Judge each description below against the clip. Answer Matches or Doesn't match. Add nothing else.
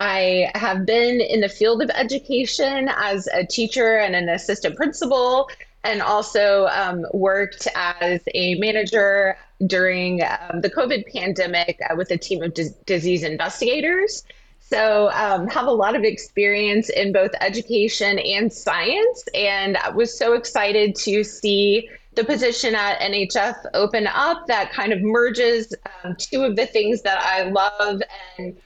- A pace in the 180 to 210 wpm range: Doesn't match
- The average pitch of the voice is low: Doesn't match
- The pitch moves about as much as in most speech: Matches